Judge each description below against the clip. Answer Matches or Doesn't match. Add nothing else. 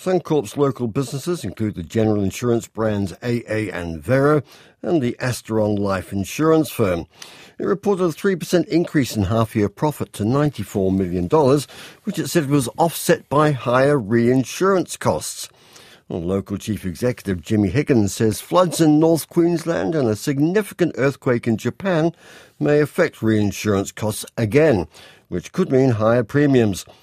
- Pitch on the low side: Matches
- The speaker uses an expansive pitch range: Matches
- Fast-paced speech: Doesn't match